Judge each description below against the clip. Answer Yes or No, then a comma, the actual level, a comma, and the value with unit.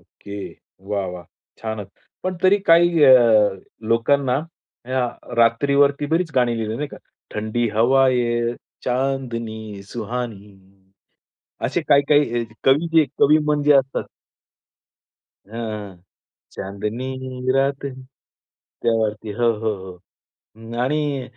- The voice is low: Yes, low, 125 Hz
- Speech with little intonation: No, average, 4.1 semitones